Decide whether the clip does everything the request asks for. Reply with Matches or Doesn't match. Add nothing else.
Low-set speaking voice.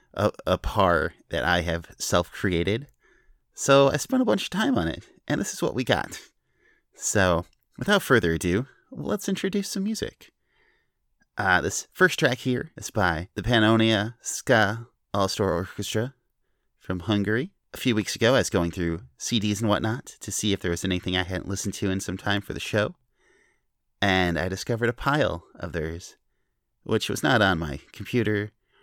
Matches